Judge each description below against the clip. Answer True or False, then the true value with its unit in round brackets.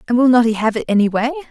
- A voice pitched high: True (235 Hz)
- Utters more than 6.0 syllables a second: True (8.0 syllables/s)